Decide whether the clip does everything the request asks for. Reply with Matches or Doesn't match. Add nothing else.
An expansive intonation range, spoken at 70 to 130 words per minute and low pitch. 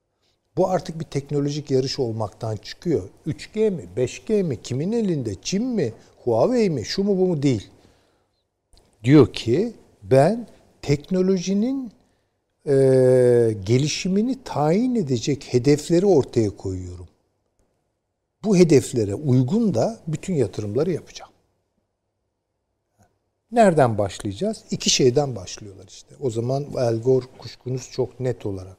Matches